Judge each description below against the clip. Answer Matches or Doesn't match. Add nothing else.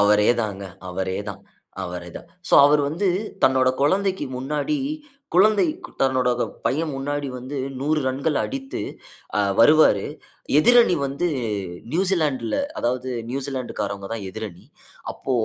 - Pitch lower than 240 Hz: Matches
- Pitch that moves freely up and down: Matches